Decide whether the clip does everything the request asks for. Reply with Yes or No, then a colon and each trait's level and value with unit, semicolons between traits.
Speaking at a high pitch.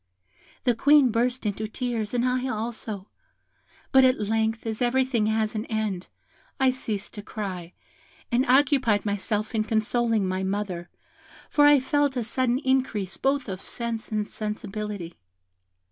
Yes: high, 225 Hz